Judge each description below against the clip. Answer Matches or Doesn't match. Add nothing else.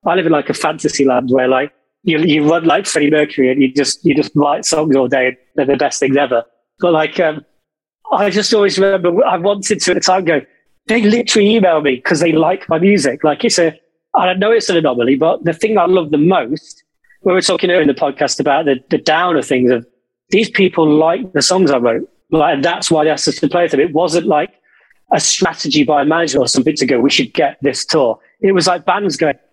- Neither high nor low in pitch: Matches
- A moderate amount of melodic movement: Matches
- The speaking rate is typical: Doesn't match